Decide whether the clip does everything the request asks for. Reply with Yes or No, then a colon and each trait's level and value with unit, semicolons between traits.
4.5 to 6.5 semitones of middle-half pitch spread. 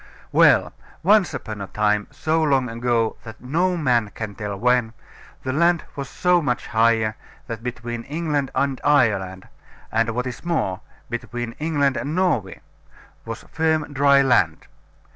Yes: average, 4.8 semitones